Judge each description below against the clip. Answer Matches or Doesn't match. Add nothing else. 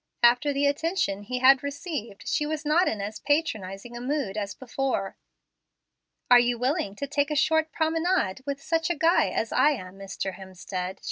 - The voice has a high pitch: Matches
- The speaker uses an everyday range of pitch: Doesn't match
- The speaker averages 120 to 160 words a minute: Doesn't match